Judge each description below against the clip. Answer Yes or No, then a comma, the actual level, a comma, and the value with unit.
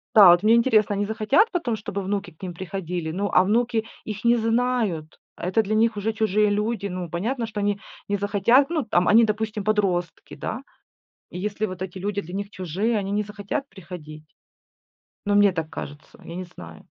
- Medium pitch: No, high, 205 Hz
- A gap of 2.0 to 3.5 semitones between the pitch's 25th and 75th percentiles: Yes, average, 3.2 semitones